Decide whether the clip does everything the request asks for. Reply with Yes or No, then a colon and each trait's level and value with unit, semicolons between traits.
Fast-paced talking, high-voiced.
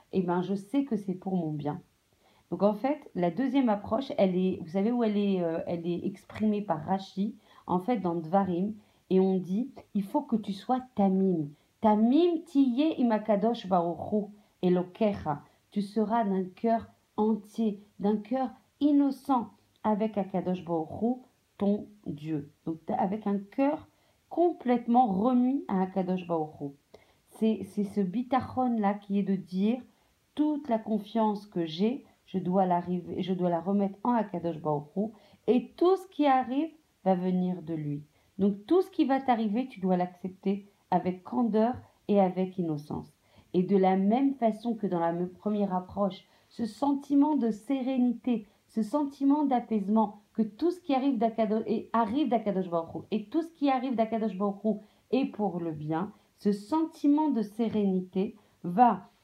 No: average, 160 wpm; high, 210 Hz